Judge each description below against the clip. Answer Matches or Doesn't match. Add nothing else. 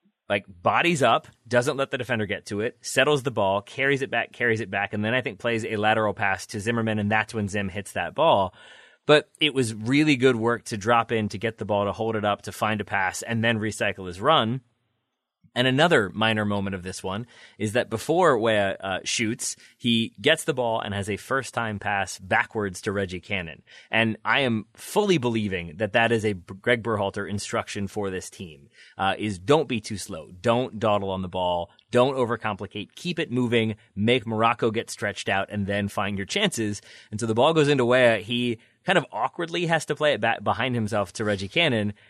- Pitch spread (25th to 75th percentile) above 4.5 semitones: Doesn't match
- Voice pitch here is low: Matches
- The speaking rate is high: Matches